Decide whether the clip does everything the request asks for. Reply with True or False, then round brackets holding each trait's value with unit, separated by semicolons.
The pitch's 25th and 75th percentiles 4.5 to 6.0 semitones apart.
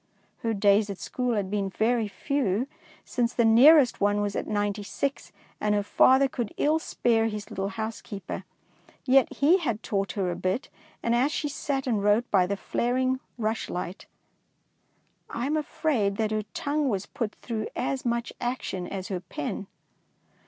False (4.1 semitones)